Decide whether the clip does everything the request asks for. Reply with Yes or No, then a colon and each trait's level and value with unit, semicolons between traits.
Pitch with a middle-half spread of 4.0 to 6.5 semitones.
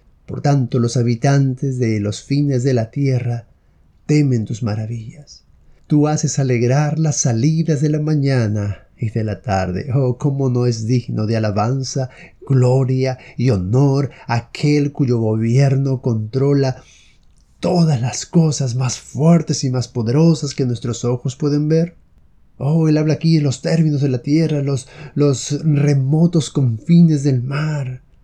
No: average, 3.6 semitones